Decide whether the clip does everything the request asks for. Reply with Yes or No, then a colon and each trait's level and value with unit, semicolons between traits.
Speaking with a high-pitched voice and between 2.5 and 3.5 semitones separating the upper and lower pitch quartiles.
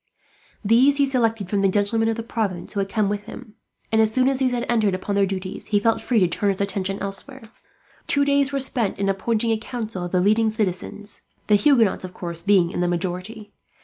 Yes: high, 210 Hz; average, 3.1 semitones